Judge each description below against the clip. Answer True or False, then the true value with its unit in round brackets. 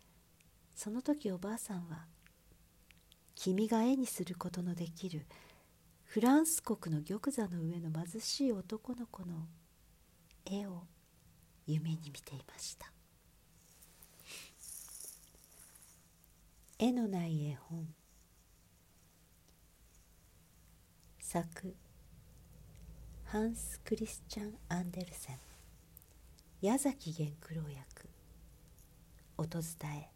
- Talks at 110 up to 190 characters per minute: True (160 characters per minute)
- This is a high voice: False (160 Hz)